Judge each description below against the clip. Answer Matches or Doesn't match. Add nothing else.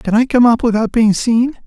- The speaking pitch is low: Doesn't match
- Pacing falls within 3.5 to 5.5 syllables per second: Matches